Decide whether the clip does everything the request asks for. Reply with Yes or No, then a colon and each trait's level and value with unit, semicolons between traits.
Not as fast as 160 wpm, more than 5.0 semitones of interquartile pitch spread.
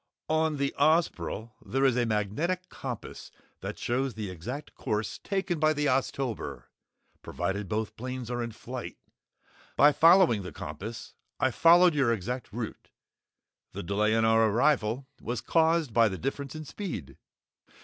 Yes: average, 150 wpm; wide, 5.5 semitones